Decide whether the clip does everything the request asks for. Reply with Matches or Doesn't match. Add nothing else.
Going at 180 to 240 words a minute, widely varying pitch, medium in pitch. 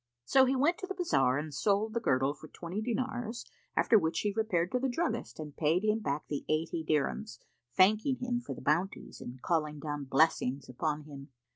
Matches